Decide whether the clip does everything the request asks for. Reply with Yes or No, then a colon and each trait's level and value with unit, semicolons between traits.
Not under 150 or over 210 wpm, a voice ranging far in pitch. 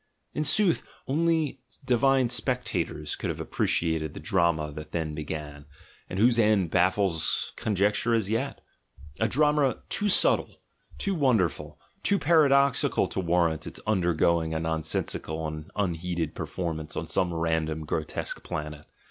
No: average, 140 wpm; wide, 7.8 semitones